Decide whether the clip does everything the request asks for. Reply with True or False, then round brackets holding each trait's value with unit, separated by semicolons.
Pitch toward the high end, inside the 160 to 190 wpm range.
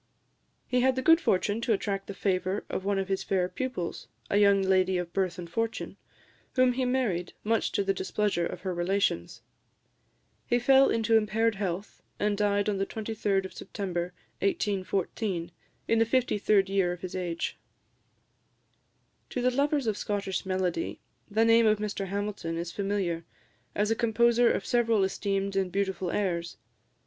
True (200 Hz; 165 wpm)